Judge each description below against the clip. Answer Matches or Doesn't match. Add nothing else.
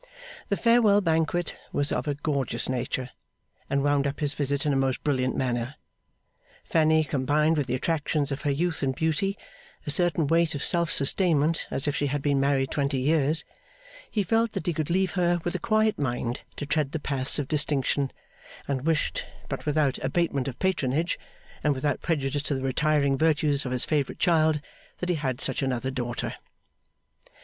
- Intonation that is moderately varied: Matches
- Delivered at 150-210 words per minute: Matches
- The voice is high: Doesn't match